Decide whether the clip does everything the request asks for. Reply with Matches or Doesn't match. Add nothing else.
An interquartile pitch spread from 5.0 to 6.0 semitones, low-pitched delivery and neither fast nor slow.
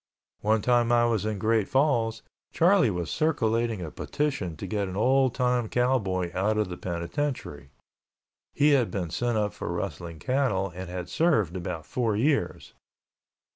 Matches